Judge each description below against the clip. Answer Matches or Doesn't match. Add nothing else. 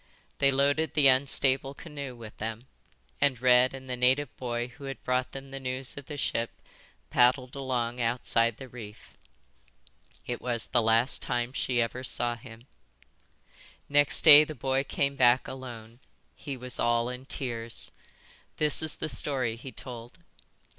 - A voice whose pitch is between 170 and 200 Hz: Doesn't match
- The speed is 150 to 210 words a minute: Matches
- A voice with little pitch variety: Matches